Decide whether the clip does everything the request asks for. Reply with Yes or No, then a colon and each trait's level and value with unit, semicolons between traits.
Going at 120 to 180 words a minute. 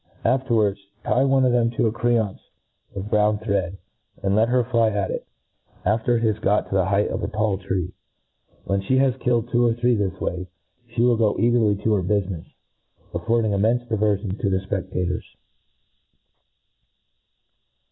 Yes: average, 165 wpm